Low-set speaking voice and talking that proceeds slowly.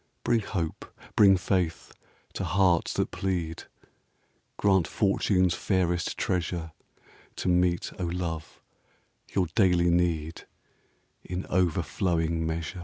Yes: very low, 90 Hz; slow, 110 wpm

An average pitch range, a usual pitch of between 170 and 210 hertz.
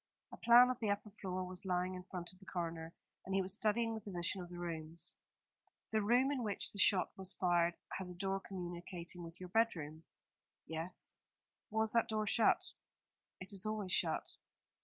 Yes: average, 3.5 semitones; medium, 185 Hz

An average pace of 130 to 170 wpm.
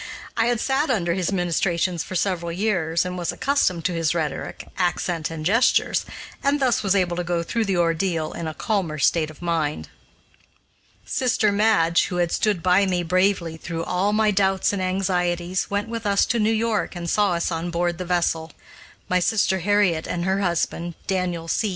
No: average, 190 wpm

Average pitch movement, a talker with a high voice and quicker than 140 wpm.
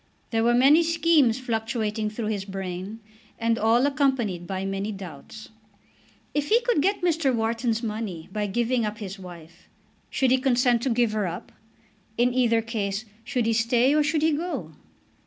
Yes: average, 3.9 semitones; high, 230 Hz; average, 170 wpm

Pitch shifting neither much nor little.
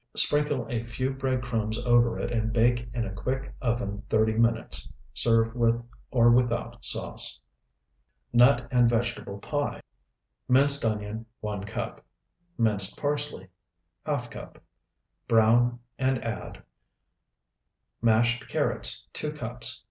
No: narrow, 2.0 semitones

